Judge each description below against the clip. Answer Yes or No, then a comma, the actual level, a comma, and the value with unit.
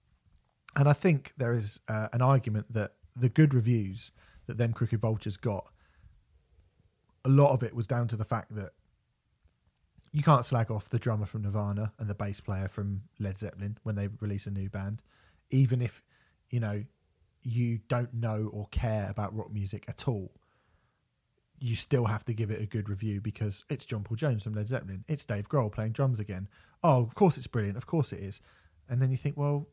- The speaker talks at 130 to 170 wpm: No, average, 200 wpm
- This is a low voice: Yes, low, 110 Hz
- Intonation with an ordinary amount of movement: Yes, average, 3.2 semitones